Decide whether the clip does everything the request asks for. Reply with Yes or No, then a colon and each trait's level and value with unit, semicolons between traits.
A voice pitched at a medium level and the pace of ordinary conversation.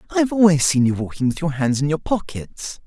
No: medium, 160 Hz; fast, 250 wpm